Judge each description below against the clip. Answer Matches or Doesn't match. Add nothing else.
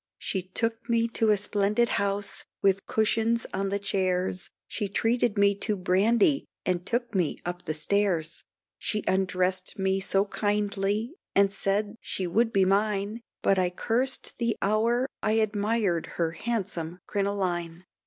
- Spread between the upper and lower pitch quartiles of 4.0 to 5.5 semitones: Doesn't match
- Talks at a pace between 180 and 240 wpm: Doesn't match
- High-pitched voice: Matches